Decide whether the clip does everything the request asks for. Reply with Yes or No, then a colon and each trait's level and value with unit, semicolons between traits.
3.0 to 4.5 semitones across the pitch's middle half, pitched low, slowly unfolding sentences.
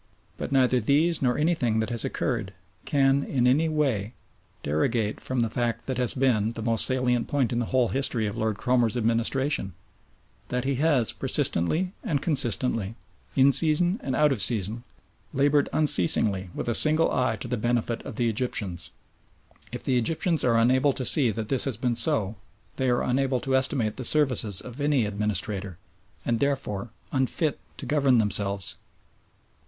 No: average, 3.6 semitones; low, 125 Hz; average, 170 wpm